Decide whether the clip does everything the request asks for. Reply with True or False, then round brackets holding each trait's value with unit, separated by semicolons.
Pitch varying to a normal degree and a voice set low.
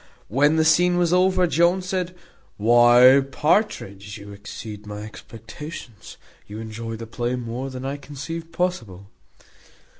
False (7.3 semitones; 125 Hz)